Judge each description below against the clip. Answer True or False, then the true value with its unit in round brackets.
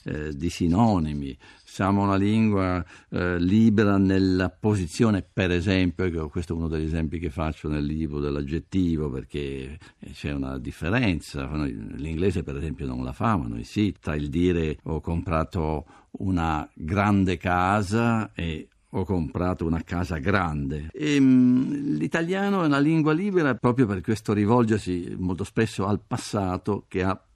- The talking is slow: False (145 wpm)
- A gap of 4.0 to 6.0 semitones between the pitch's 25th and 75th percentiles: True (4.8 semitones)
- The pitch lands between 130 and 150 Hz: False (90 Hz)